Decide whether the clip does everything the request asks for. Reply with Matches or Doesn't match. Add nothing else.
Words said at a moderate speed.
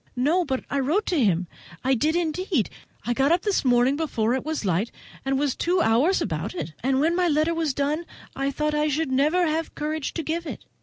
Doesn't match